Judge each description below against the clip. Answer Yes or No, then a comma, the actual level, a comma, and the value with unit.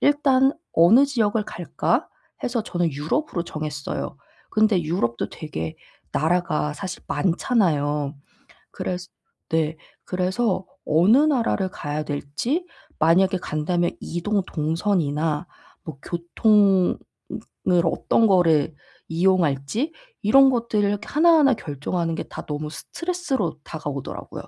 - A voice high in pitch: No, medium, 180 Hz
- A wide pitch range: Yes, wide, 6.0 semitones